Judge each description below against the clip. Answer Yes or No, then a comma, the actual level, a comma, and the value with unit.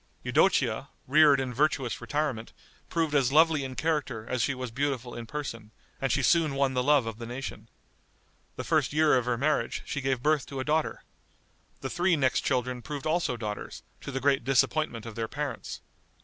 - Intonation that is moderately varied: Yes, average, 3.3 semitones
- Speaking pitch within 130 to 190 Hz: Yes, low, 135 Hz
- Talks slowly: No, average, 190 wpm